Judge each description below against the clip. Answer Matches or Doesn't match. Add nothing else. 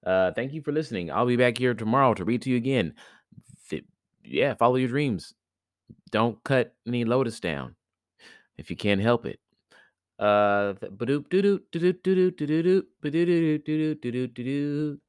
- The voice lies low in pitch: Matches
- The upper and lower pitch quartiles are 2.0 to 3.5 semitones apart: Doesn't match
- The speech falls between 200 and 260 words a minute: Doesn't match